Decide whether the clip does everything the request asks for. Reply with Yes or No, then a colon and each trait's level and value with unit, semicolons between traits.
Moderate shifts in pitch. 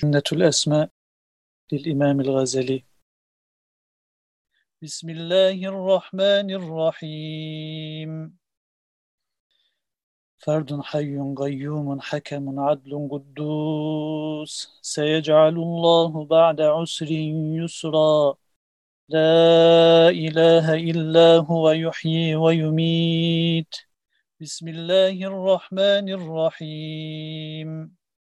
No: narrow, 1.8 semitones